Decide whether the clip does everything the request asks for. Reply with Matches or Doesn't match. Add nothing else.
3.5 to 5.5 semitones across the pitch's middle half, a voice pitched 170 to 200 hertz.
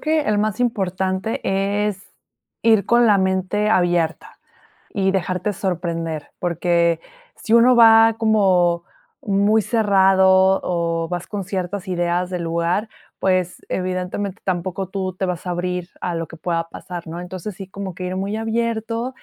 Doesn't match